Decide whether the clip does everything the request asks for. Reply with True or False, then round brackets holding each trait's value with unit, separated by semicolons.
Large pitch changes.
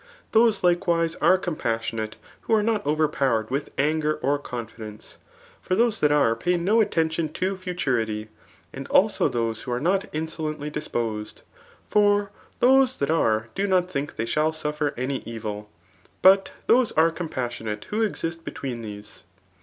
True (7.7 semitones)